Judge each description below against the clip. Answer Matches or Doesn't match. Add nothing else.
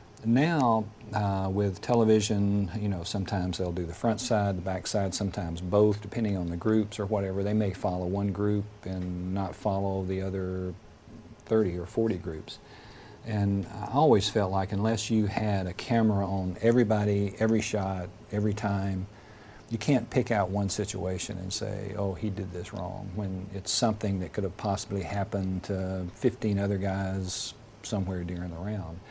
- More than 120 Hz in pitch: Doesn't match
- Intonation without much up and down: Matches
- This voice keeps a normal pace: Matches